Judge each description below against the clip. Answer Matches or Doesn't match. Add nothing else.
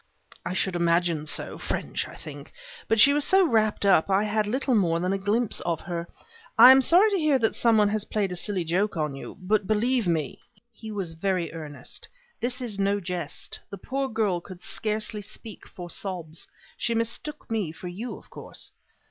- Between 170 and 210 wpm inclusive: Matches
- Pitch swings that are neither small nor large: Matches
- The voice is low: Doesn't match